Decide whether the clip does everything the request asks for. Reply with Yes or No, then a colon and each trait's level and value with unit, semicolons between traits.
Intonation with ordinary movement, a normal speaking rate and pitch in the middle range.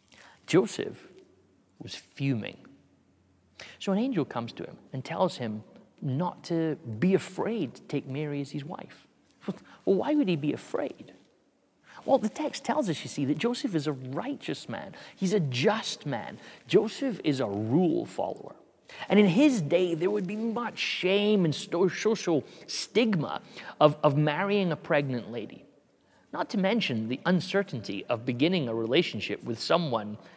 No: wide, 7.2 semitones; average, 155 wpm; medium, 160 Hz